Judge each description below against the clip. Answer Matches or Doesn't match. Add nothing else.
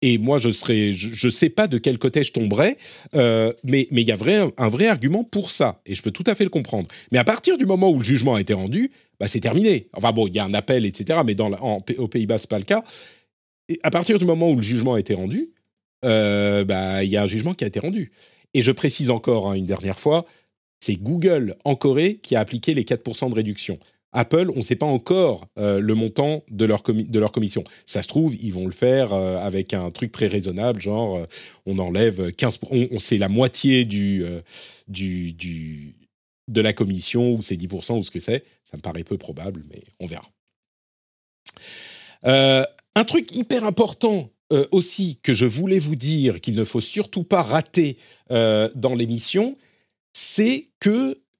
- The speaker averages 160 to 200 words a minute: Doesn't match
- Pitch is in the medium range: Doesn't match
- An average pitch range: Doesn't match